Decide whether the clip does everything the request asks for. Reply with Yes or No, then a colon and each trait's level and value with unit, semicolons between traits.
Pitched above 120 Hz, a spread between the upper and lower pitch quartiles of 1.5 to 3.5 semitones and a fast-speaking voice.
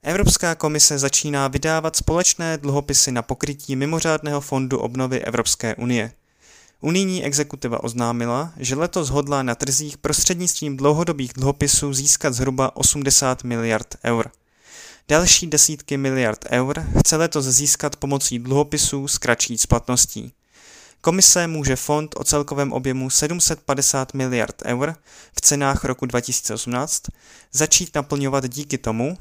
No: medium, 140 Hz; average, 2.7 semitones; average, 120 wpm